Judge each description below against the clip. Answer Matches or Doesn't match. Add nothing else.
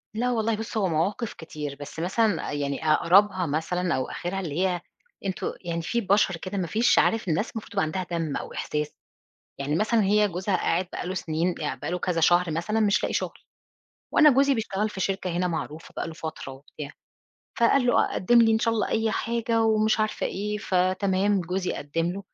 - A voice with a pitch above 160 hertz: Matches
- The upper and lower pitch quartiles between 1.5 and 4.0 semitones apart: Doesn't match